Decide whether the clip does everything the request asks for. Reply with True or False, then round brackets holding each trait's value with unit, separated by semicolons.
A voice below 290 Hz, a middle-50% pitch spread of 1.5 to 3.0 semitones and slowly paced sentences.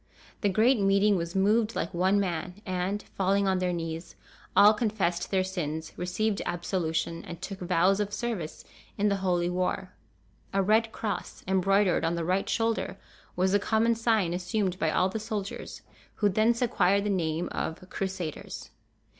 False (190 Hz; 2.7 semitones; 165 wpm)